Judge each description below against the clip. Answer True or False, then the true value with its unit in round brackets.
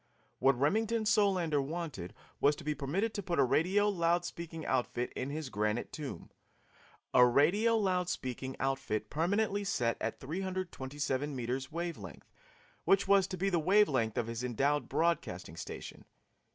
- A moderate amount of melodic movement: False (6.3 semitones)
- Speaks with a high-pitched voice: False (155 Hz)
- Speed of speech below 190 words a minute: True (155 wpm)